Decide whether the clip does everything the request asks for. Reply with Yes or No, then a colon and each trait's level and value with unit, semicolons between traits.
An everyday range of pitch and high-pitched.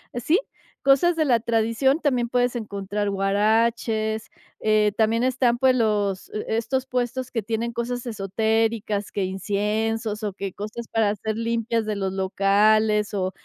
No: narrow, 2.3 semitones; high, 220 Hz